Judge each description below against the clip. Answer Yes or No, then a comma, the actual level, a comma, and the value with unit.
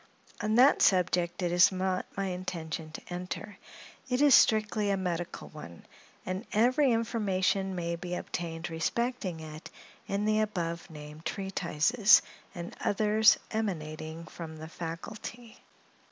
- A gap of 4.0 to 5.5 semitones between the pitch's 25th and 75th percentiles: Yes, average, 4.3 semitones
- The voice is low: No, medium, 185 Hz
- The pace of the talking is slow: Yes, slow, 130 wpm